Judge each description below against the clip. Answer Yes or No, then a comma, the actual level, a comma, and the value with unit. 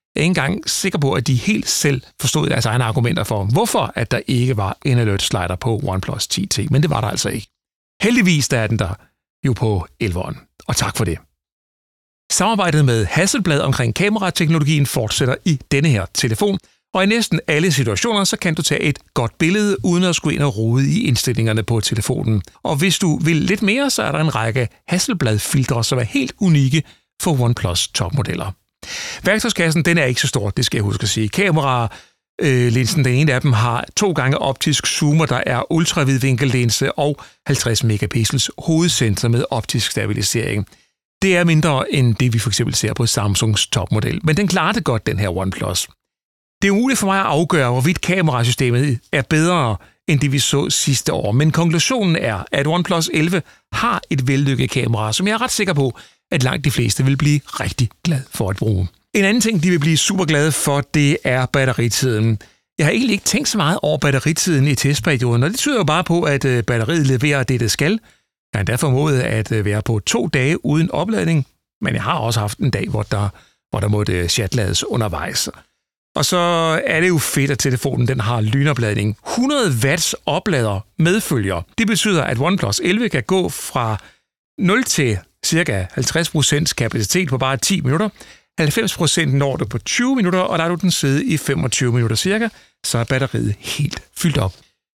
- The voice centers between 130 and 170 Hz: Yes, medium, 140 Hz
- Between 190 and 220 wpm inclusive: Yes, average, 195 wpm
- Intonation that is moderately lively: No, wide, 6.2 semitones